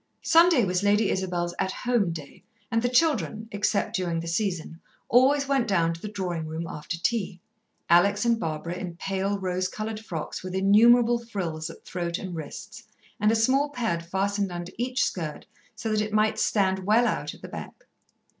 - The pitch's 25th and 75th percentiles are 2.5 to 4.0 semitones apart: No, average, 4.6 semitones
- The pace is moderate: Yes, average, 185 wpm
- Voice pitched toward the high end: Yes, high, 195 Hz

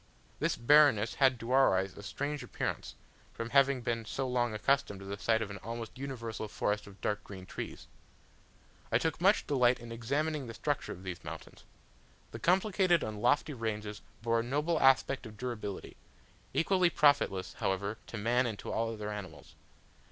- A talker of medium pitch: No, low, 115 Hz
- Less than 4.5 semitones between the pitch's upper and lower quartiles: No, average, 4.8 semitones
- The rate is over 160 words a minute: Yes, average, 175 wpm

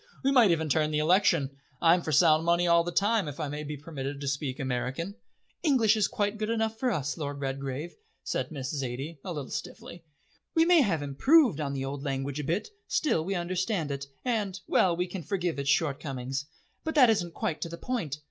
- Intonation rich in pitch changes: Yes, wide, 5.8 semitones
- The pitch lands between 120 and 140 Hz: No, medium, 165 Hz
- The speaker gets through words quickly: Yes, fast, 210 wpm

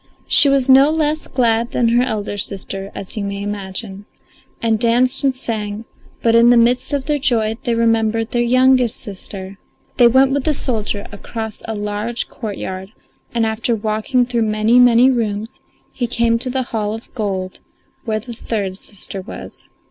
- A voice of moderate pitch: No, high, 230 Hz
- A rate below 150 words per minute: No, average, 170 wpm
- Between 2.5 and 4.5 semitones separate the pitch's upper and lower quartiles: Yes, average, 3.0 semitones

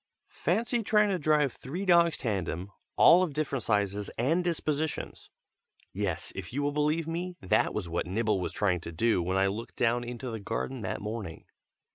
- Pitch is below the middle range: Yes, low, 120 Hz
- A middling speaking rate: Yes, average, 180 wpm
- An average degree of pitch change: No, wide, 8.0 semitones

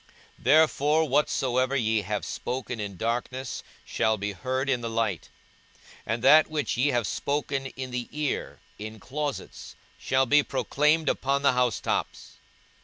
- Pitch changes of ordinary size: Yes, average, 4.0 semitones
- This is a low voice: Yes, low, 130 Hz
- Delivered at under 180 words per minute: Yes, average, 145 wpm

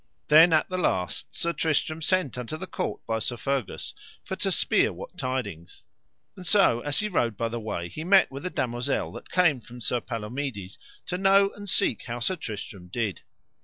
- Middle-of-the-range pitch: No, low, 130 Hz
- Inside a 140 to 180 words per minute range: No, average, 195 wpm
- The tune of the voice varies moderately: No, wide, 6.9 semitones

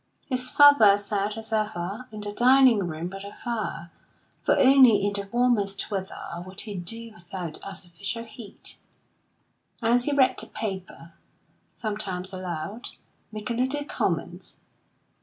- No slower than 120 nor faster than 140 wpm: Yes, slow, 135 wpm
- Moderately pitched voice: No, high, 210 Hz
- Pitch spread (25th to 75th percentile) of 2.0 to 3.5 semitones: No, average, 4.0 semitones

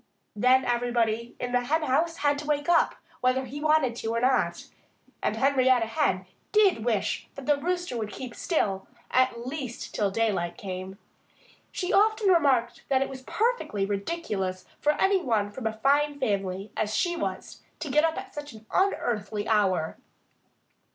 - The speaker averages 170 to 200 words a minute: No, average, 160 wpm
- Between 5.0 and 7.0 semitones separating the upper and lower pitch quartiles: Yes, wide, 5.6 semitones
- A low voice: No, very high, 255 Hz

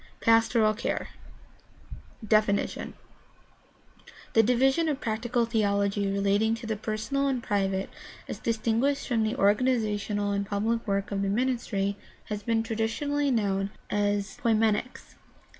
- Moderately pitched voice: No, high, 220 Hz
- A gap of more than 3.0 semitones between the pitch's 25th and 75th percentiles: No, narrow, 2.5 semitones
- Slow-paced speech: Yes, slow, 125 wpm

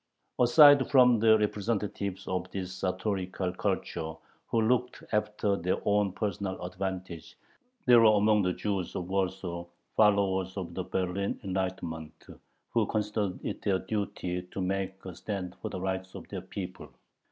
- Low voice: Yes, very low, 95 Hz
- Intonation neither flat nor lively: No, narrow, 2.3 semitones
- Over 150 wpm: No, average, 145 wpm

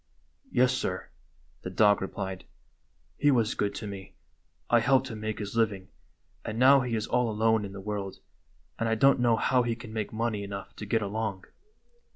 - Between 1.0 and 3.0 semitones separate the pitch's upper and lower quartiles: Yes, average, 2.7 semitones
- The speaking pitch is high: No, low, 110 Hz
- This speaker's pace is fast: No, average, 195 wpm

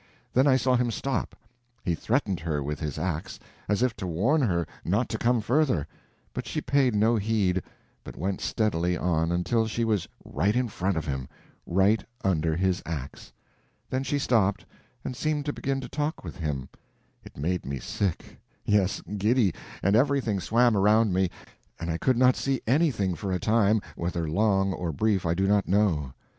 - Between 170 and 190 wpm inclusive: Yes, average, 175 wpm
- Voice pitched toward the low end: Yes, low, 100 Hz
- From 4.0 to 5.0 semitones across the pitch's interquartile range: No, wide, 5.6 semitones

